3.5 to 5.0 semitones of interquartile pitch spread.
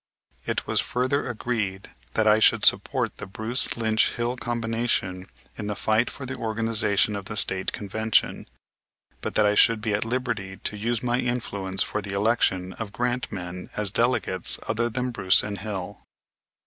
No: average, 3.0 semitones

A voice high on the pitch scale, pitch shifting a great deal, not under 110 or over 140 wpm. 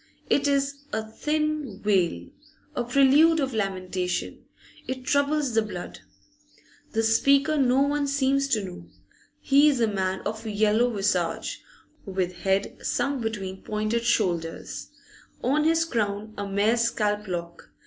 Yes: high, 225 Hz; wide, 5.9 semitones; slow, 135 wpm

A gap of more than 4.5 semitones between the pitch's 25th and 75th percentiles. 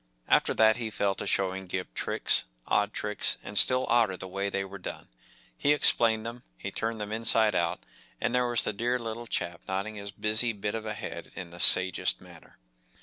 No: average, 3.0 semitones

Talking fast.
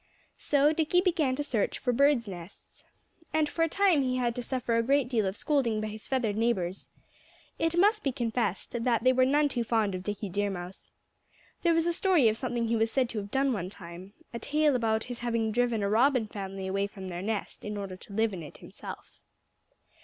Yes: fast, 220 wpm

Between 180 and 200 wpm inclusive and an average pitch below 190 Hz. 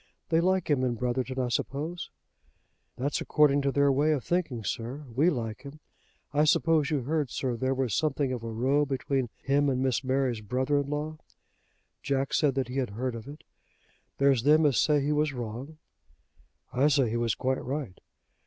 Yes: average, 190 wpm; low, 135 Hz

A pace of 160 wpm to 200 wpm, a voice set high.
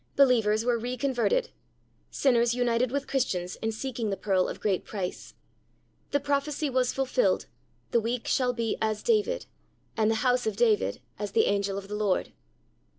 Yes: average, 165 wpm; high, 235 Hz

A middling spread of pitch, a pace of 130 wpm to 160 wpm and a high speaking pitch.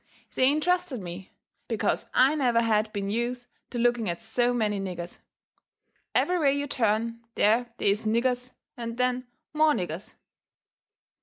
Yes: average, 3.2 semitones; average, 145 wpm; high, 235 Hz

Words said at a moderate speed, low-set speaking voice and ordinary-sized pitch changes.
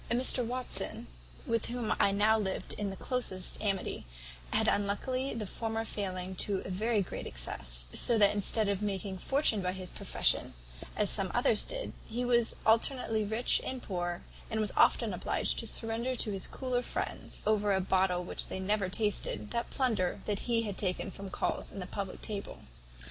No: average, 180 wpm; high, 210 Hz; average, 3.3 semitones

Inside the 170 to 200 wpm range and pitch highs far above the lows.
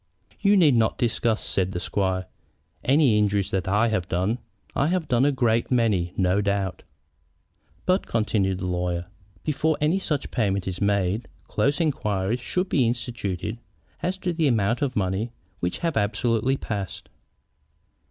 No: average, 150 wpm; wide, 5.9 semitones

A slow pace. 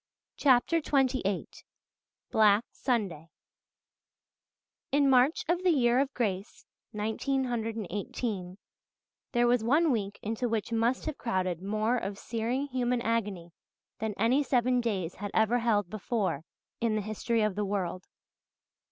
Yes: slow, 125 wpm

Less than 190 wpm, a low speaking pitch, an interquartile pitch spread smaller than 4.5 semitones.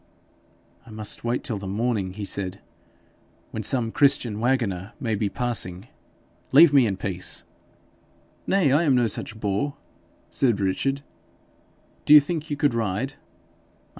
No: average, 140 wpm; low, 115 Hz; average, 5.3 semitones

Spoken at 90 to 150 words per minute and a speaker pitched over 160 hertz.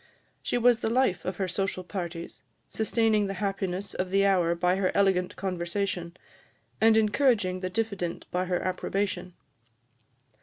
Yes: average, 145 wpm; high, 190 Hz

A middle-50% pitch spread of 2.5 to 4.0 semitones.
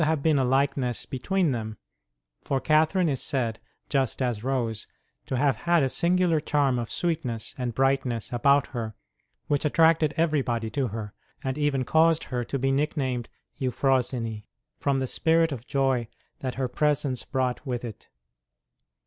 Yes: average, 3.5 semitones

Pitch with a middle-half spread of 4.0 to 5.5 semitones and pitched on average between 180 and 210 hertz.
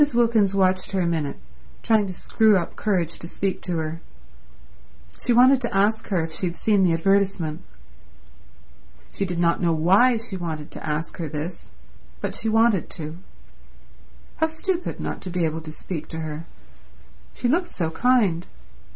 Yes: average, 5.0 semitones; medium, 185 Hz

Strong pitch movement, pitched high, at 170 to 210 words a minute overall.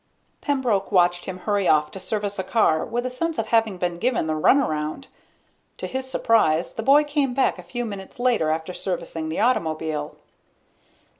Yes: wide, 7.0 semitones; high, 195 Hz; average, 175 wpm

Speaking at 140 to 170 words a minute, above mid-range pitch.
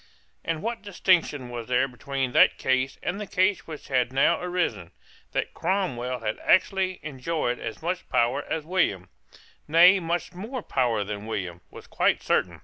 No: average, 160 wpm; medium, 145 Hz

